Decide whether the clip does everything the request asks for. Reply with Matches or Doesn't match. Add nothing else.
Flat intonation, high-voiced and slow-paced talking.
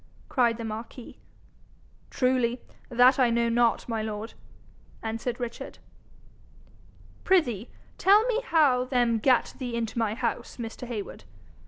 Matches